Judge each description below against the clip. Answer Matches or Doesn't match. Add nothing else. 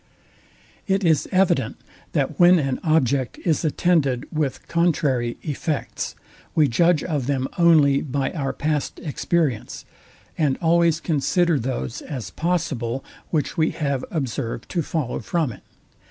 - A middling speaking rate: Doesn't match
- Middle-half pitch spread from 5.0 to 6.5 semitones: Doesn't match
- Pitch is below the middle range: Doesn't match